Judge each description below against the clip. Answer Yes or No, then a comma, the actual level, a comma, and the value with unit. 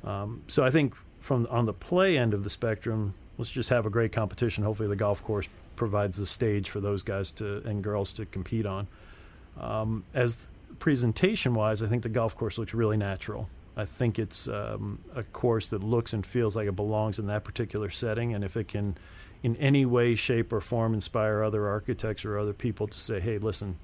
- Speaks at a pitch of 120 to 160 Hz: No, low, 110 Hz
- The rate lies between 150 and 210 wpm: Yes, fast, 205 wpm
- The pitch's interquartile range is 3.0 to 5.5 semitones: No, narrow, 2.4 semitones